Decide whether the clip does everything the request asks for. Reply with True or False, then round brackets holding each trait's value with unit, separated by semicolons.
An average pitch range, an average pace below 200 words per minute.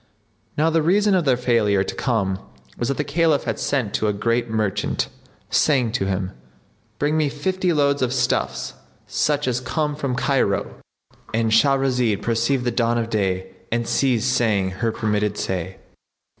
True (4.9 semitones; 160 wpm)